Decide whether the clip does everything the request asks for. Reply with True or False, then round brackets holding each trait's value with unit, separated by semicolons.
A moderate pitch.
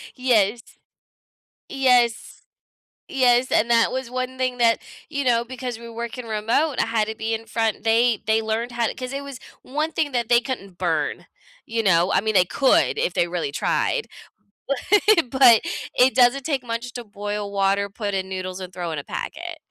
False (230 Hz)